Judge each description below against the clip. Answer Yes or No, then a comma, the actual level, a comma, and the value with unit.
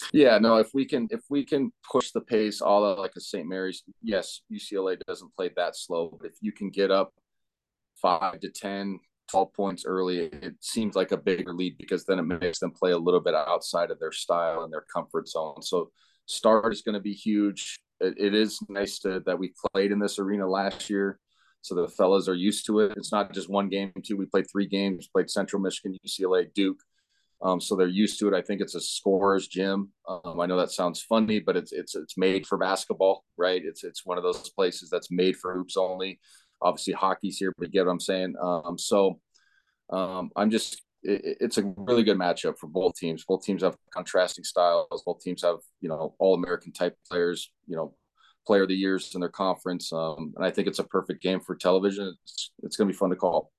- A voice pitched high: No, very low, 95 Hz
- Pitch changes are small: Yes, narrow, 2.0 semitones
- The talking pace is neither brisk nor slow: No, fast, 225 wpm